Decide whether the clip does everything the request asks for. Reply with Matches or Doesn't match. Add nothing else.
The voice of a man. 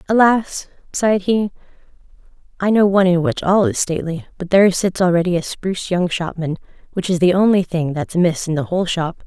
Doesn't match